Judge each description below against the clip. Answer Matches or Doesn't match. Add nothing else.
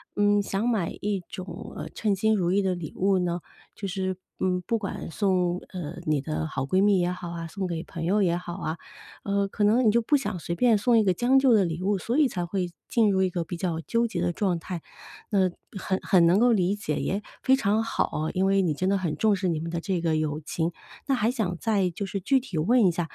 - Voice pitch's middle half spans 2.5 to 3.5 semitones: Matches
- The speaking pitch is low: Doesn't match